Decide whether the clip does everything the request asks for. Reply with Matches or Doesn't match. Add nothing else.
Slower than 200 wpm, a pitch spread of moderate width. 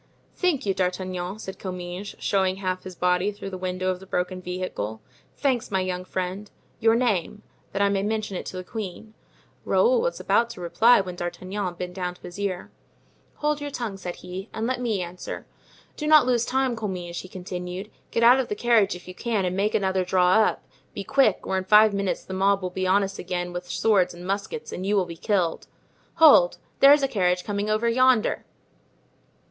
Doesn't match